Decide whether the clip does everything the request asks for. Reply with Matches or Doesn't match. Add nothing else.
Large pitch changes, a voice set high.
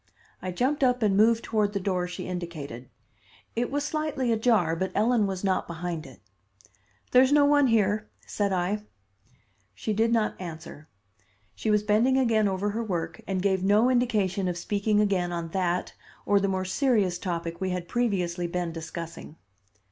Doesn't match